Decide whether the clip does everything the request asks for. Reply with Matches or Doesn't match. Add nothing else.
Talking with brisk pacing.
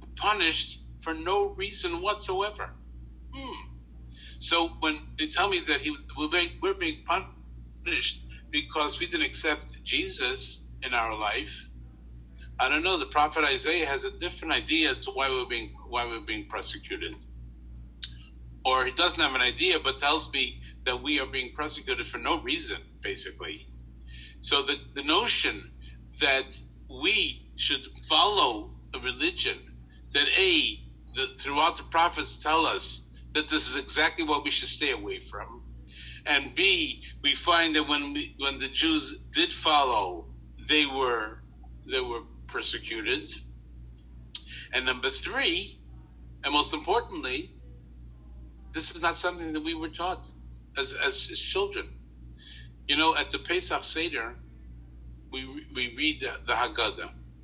Doesn't match